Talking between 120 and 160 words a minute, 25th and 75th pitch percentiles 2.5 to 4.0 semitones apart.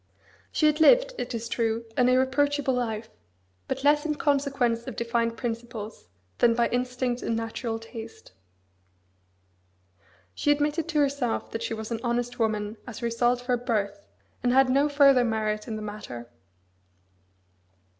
Yes: average, 155 wpm; average, 3.0 semitones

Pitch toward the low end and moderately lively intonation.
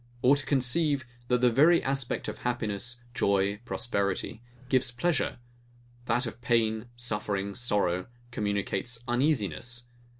Yes: low, 120 Hz; average, 3.6 semitones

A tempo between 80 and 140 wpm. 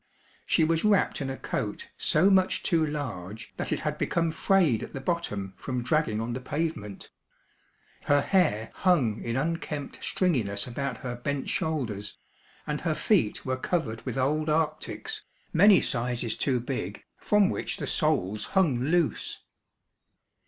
No: average, 150 wpm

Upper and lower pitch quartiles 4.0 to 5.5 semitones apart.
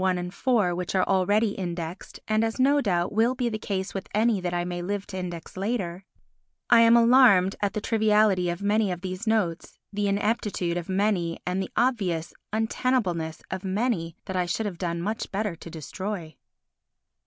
No: average, 3.6 semitones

